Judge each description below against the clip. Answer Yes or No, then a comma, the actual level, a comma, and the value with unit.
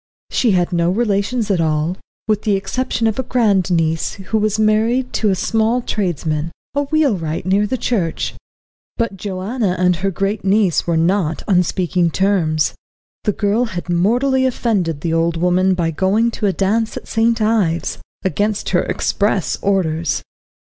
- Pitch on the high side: Yes, high, 195 Hz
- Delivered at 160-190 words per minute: Yes, average, 165 wpm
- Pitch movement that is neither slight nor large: Yes, average, 4.1 semitones